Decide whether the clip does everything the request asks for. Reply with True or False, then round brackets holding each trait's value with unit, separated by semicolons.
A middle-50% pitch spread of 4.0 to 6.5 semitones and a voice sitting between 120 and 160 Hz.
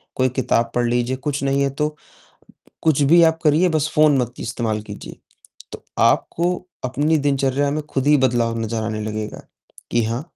True (4.3 semitones; 135 Hz)